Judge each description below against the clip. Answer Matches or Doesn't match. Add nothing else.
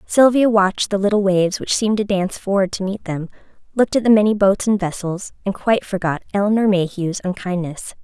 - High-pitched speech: Matches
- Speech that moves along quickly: Doesn't match